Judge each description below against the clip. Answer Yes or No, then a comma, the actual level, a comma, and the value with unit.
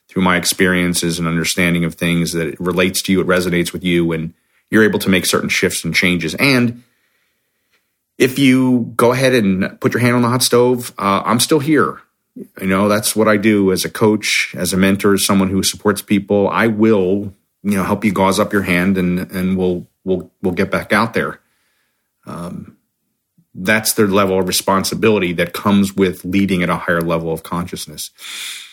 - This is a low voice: Yes, very low, 95 Hz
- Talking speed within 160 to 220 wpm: Yes, average, 195 wpm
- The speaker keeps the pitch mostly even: No, average, 3.3 semitones